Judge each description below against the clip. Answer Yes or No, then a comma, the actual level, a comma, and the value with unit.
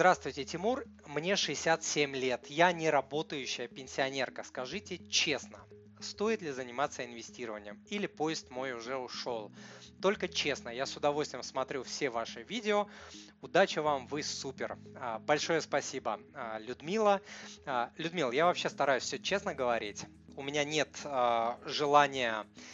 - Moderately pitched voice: Yes, medium, 145 Hz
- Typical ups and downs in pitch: No, wide, 6.0 semitones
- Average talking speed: Yes, average, 125 wpm